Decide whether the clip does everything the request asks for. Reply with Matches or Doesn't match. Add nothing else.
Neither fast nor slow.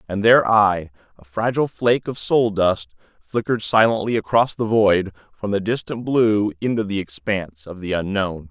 Matches